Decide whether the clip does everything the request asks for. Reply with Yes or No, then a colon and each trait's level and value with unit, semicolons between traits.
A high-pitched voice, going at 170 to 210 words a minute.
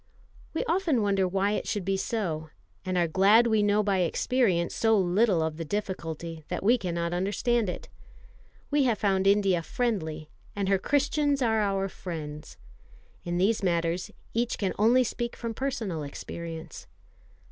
No: high, 195 Hz; average, 160 wpm